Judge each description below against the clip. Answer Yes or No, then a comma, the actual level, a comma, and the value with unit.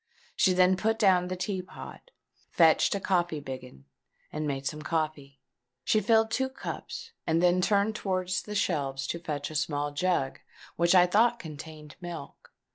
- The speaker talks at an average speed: Yes, average, 165 wpm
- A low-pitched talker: No, medium, 175 Hz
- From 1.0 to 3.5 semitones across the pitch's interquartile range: No, average, 4.1 semitones